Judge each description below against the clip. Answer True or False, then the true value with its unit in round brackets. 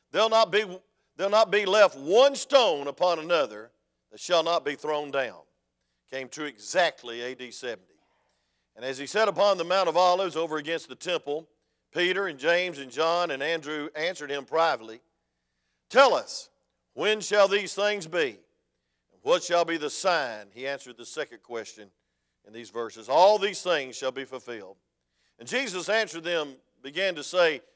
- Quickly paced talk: False (165 wpm)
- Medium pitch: True (160 Hz)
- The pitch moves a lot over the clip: True (6.9 semitones)